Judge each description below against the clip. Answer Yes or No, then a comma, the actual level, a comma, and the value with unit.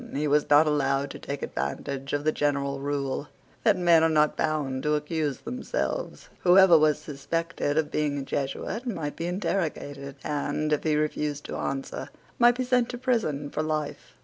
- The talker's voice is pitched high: No, medium, 150 Hz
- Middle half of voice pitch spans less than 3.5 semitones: Yes, average, 2.9 semitones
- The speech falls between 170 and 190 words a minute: Yes, average, 175 wpm